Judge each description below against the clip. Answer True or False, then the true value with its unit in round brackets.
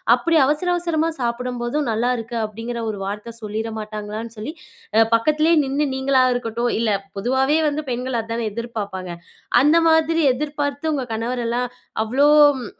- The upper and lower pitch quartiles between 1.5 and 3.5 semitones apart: False (4.3 semitones)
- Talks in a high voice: True (245 Hz)